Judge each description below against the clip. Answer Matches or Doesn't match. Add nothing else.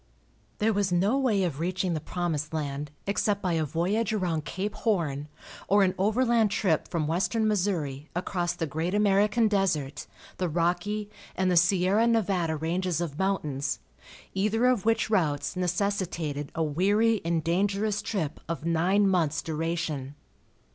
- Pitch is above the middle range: Doesn't match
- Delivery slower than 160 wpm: Matches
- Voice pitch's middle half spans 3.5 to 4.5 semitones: Matches